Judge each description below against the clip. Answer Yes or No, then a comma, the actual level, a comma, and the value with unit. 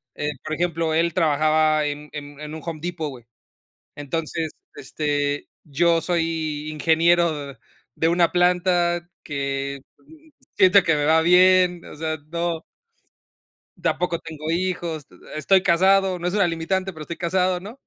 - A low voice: No, medium, 165 Hz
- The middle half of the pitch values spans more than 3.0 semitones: No, narrow, 2.5 semitones